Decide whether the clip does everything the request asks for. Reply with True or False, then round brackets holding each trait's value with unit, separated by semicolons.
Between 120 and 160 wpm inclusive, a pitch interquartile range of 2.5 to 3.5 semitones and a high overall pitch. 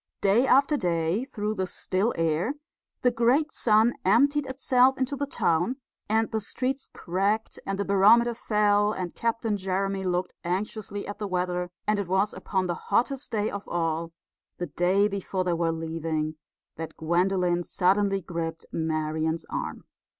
False (155 wpm; 4.4 semitones; 195 Hz)